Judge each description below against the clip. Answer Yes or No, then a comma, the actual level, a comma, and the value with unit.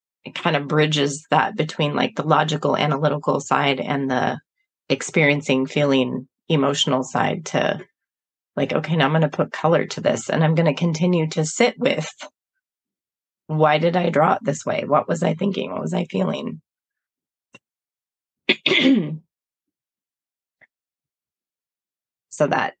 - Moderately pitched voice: Yes, medium, 155 Hz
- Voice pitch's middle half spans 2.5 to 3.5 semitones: Yes, average, 3.1 semitones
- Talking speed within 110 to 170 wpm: Yes, average, 140 wpm